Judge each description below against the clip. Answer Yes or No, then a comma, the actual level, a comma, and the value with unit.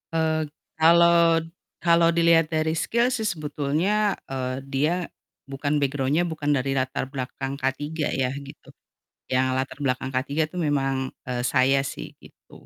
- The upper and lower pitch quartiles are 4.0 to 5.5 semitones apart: No, average, 3.3 semitones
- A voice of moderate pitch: Yes, medium, 145 Hz